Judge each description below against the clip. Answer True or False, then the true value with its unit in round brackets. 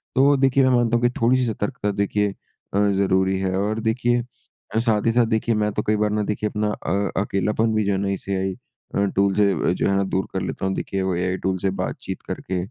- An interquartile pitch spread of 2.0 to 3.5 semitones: True (2.6 semitones)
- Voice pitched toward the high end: False (105 Hz)